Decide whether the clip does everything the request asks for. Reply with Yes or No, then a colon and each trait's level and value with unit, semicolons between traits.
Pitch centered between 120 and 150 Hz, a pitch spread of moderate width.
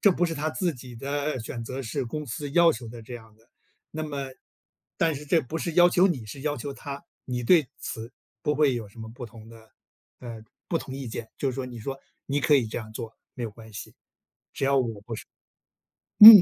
Yes: low, 135 Hz; average, 4.7 semitones